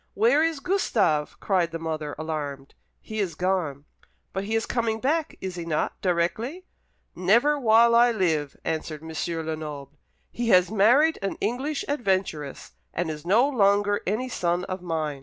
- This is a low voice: No, high, 190 Hz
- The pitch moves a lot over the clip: Yes, wide, 6.6 semitones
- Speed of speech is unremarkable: Yes, average, 160 wpm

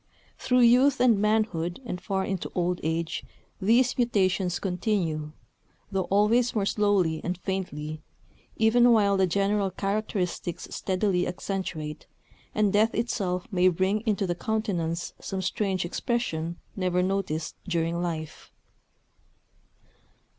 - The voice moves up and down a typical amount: Yes, average, 3.3 semitones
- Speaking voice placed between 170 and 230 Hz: Yes, high, 190 Hz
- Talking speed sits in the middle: No, slow, 120 wpm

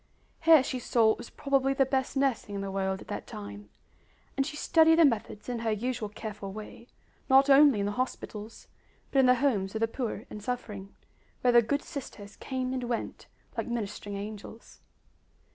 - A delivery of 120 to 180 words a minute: No, average, 190 wpm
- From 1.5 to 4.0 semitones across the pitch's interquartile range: No, average, 4.4 semitones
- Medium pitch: No, high, 235 Hz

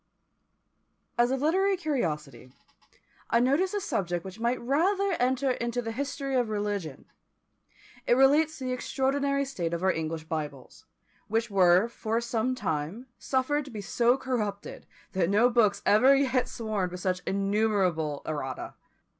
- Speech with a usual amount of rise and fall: No, wide, 6.2 semitones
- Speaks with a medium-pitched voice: No, high, 230 Hz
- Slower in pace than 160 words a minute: Yes, average, 145 wpm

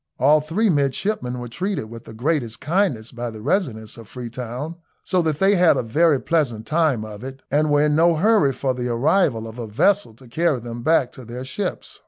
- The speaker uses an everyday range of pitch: No, wide, 5.8 semitones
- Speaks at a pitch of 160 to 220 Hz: No, low, 135 Hz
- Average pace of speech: No, fast, 210 wpm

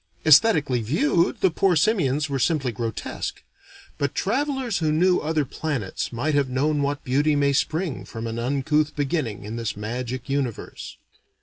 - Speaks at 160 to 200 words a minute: No, average, 150 wpm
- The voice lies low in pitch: No, medium, 145 Hz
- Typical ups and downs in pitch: Yes, average, 3.9 semitones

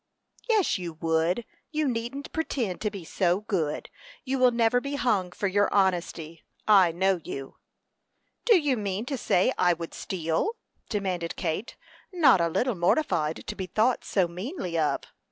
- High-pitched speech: Yes, high, 195 Hz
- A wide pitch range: Yes, wide, 6.3 semitones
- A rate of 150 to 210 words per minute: Yes, average, 160 wpm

